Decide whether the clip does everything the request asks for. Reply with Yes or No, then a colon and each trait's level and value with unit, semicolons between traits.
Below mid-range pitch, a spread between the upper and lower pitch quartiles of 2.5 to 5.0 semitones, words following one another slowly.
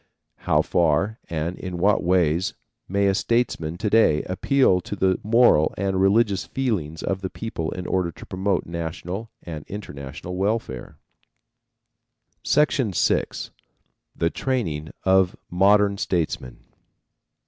Yes: very low, 95 Hz; average, 3.5 semitones; slow, 120 wpm